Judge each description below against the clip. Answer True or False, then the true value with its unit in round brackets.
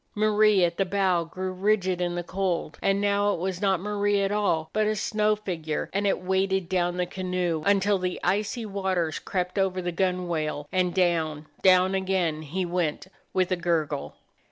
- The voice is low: False (185 Hz)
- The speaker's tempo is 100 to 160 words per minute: False (180 wpm)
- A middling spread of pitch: False (2.2 semitones)